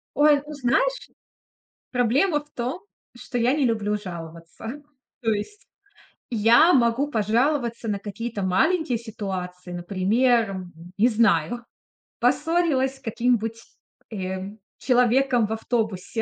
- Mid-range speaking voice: No, high, 235 Hz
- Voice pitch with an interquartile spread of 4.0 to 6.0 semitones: Yes, average, 4.3 semitones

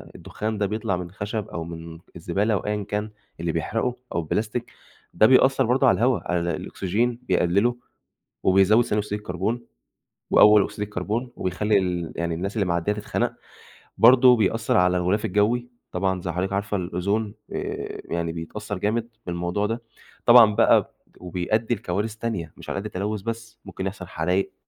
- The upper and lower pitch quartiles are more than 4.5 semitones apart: No, average, 3.7 semitones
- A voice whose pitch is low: Yes, low, 100 Hz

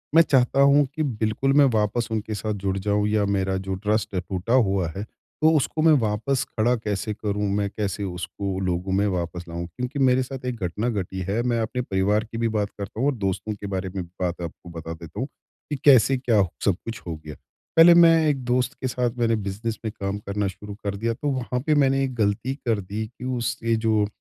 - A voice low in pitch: Yes, low, 110 Hz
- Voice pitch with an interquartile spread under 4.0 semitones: No, average, 4.3 semitones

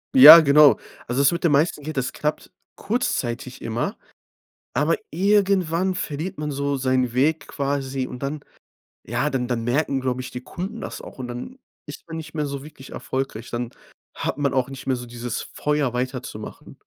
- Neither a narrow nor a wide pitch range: Yes, average, 3.5 semitones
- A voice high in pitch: No, medium, 140 Hz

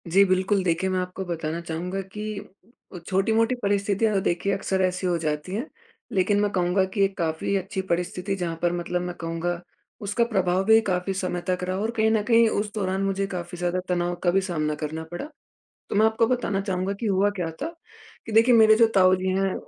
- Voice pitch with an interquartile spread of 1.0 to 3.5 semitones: Yes, narrow, 2.5 semitones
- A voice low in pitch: No, high, 190 Hz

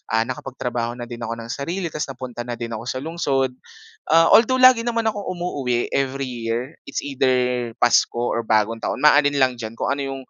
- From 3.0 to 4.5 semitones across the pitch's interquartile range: Yes, average, 3.8 semitones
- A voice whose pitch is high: No, low, 130 Hz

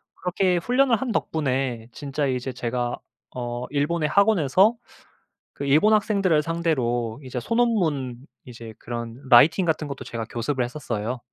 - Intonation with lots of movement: Yes, wide, 6.2 semitones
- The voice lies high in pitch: No, medium, 140 Hz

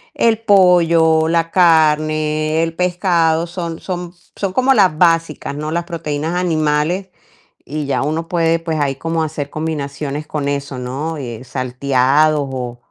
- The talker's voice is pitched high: No, medium, 160 Hz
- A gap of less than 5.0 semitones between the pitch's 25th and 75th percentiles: Yes, average, 2.7 semitones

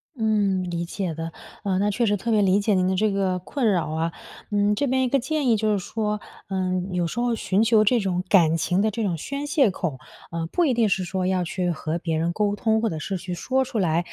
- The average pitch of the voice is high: Yes, high, 195 Hz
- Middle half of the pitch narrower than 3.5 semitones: No, average, 3.8 semitones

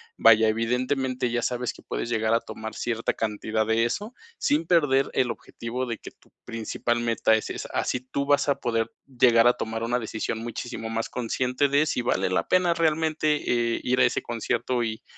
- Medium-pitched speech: No, low, 120 Hz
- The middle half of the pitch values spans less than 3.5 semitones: Yes, narrow, 2.6 semitones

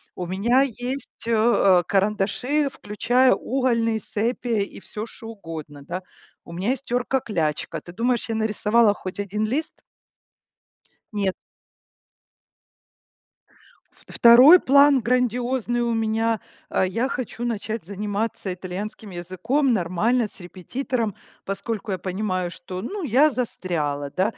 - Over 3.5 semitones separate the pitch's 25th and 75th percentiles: Yes, average, 4.5 semitones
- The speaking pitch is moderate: No, high, 220 Hz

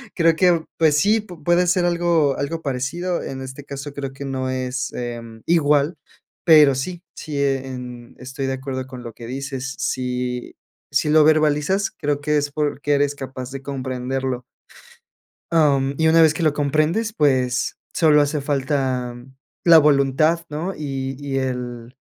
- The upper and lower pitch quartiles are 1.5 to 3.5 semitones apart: Yes, average, 3.1 semitones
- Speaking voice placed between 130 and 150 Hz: Yes, medium, 140 Hz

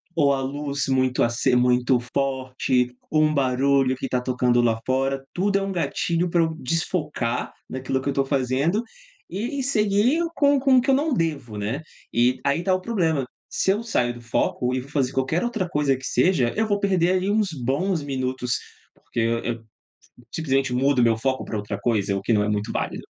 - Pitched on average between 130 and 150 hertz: Yes, low, 135 Hz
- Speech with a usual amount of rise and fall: No, wide, 6.2 semitones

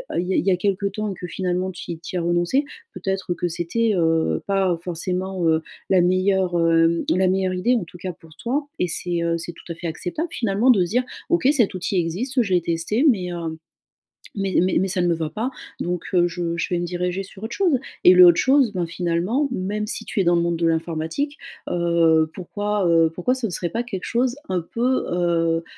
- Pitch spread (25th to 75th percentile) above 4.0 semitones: No, average, 3.2 semitones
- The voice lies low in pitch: No, medium, 180 Hz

